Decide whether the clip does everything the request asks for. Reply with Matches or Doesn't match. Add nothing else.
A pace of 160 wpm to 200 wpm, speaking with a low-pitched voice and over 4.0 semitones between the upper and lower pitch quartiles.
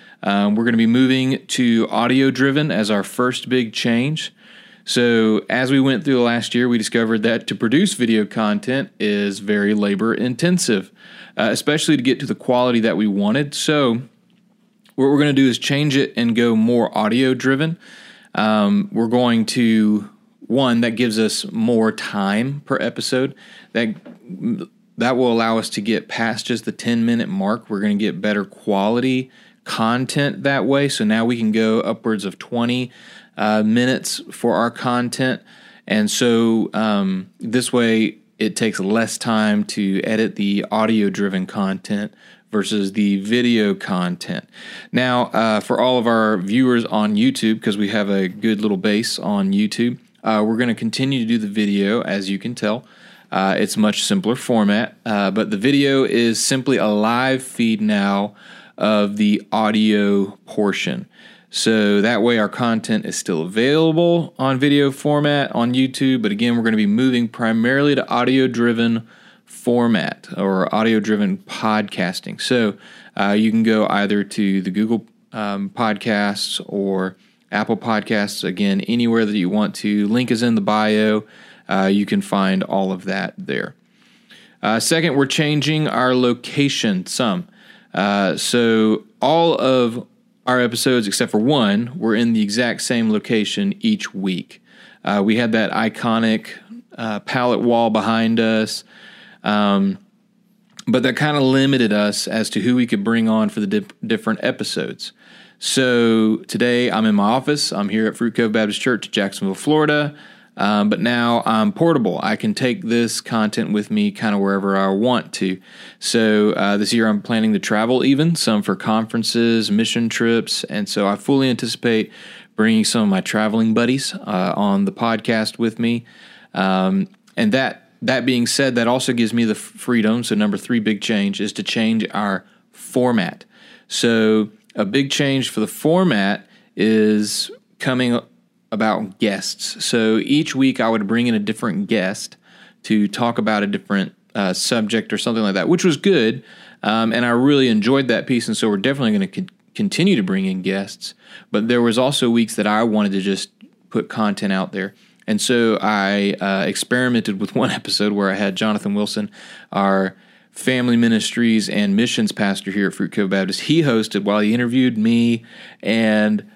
Matches